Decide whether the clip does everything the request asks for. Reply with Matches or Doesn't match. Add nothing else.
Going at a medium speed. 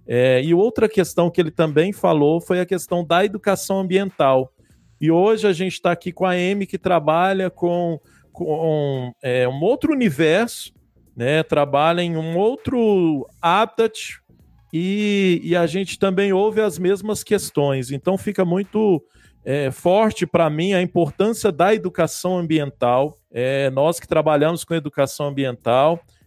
Matches